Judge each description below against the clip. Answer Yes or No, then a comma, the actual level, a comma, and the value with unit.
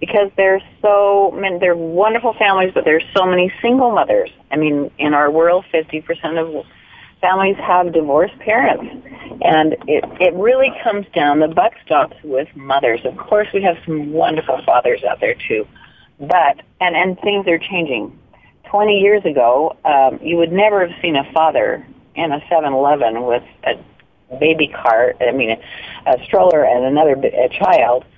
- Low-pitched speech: No, medium, 180 Hz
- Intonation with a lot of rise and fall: No, average, 4.5 semitones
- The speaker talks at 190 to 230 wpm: No, average, 165 wpm